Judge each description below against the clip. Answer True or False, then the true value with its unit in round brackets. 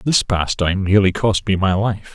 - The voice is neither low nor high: False (100 Hz)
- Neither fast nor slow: True (195 wpm)